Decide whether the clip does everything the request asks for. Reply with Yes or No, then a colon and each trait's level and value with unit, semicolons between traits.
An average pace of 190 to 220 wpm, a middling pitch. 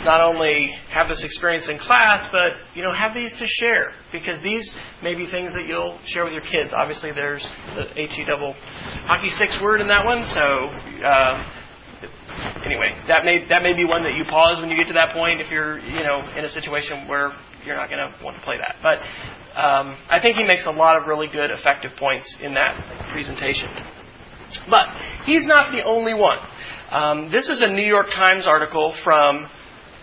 Yes: fast, 205 wpm; medium, 165 Hz